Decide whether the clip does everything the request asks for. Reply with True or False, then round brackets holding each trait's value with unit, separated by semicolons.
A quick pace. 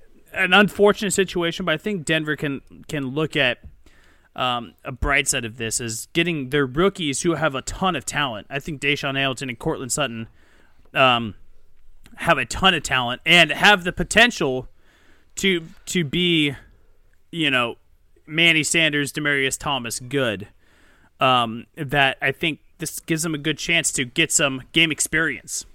False (160 wpm)